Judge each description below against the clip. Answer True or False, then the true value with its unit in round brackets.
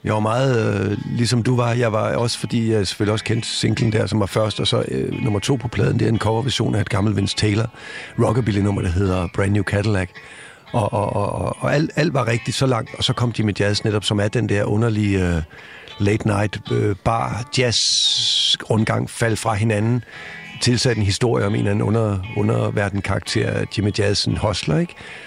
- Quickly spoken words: False (190 wpm)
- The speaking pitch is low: True (110 Hz)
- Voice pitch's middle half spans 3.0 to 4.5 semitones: False (2.5 semitones)